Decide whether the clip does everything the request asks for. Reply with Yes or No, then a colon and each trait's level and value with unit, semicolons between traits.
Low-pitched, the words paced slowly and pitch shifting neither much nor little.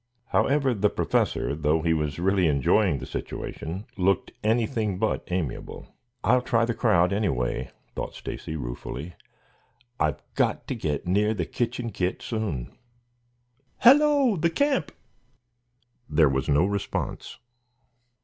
No: very low, 95 Hz; slow, 125 wpm; wide, 6.9 semitones